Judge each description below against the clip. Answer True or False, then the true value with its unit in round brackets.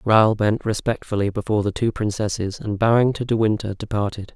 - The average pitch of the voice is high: False (105 Hz)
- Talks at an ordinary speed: True (180 wpm)